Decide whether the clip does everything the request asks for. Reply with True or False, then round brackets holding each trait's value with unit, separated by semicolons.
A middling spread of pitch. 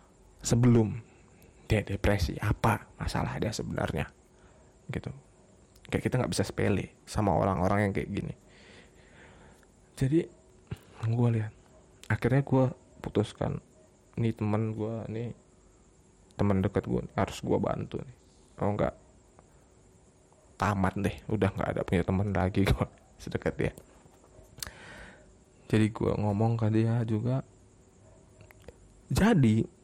True (3.5 semitones)